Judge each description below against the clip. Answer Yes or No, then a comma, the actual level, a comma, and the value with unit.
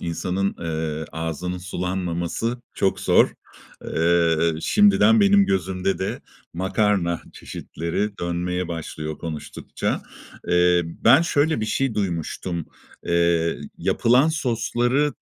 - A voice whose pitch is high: No, very low, 90 Hz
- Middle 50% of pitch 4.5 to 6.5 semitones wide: Yes, average, 5.1 semitones